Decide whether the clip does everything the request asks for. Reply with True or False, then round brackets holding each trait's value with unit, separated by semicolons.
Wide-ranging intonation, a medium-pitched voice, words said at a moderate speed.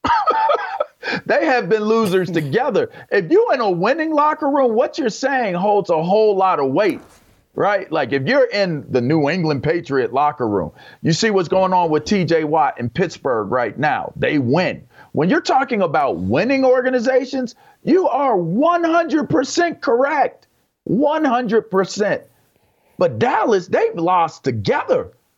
False (8.4 semitones; 225 Hz; 145 wpm)